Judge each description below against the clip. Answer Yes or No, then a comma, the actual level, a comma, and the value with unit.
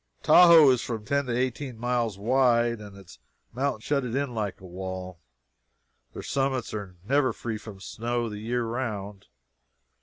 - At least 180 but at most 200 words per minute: No, average, 160 wpm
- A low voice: Yes, low, 120 Hz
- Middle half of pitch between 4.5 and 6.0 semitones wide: No, average, 3.8 semitones